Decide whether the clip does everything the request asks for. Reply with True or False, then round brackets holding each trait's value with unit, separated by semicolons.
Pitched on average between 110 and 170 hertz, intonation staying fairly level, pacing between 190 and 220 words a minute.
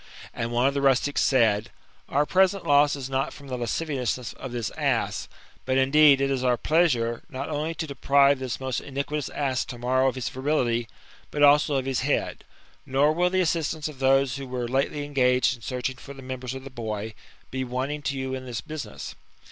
True (135 Hz; 2.3 semitones; 205 wpm)